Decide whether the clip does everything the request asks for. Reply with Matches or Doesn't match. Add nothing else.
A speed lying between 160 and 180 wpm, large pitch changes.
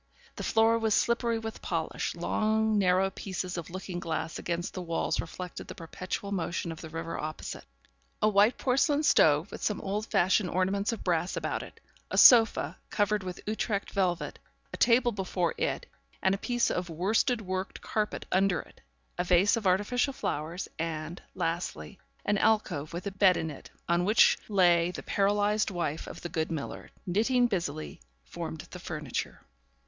Doesn't match